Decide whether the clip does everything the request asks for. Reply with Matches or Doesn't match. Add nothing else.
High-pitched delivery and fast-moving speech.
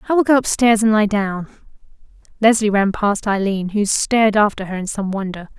Doesn't match